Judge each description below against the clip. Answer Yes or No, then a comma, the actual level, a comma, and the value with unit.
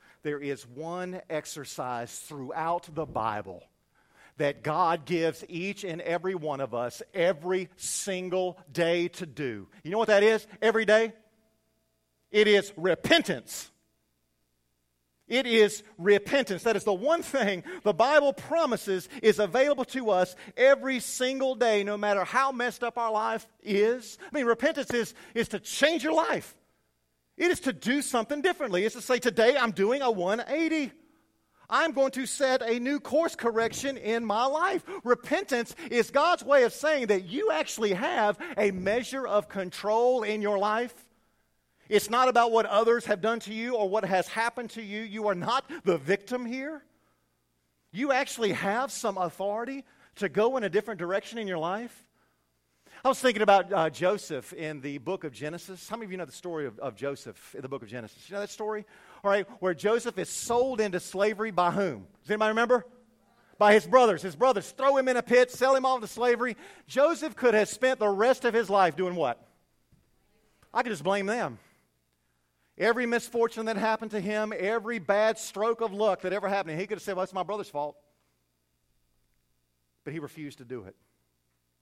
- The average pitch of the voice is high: Yes, high, 210 Hz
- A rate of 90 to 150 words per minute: No, average, 185 wpm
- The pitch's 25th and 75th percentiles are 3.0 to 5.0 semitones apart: No, wide, 5.5 semitones